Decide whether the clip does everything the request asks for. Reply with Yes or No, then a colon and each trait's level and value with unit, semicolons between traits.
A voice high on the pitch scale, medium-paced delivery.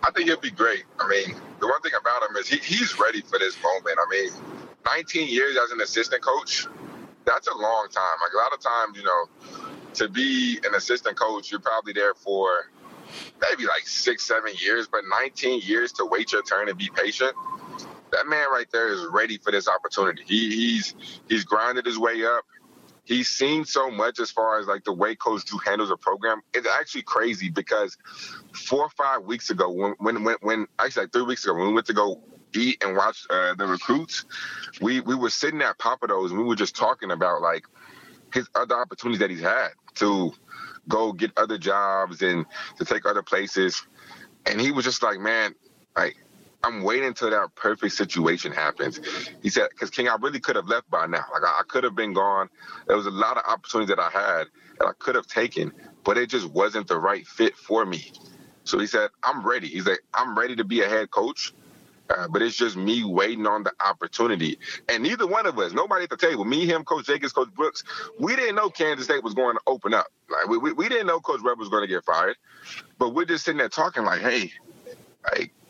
No: very high, 270 Hz; fast, 220 wpm